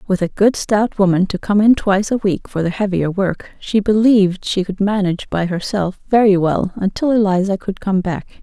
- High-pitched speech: Yes, high, 195 Hz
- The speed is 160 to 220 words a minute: Yes, fast, 205 wpm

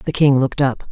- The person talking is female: Yes, female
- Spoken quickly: Yes, fast, 265 wpm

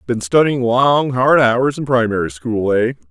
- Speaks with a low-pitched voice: Yes, low, 120 Hz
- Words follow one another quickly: No, average, 175 wpm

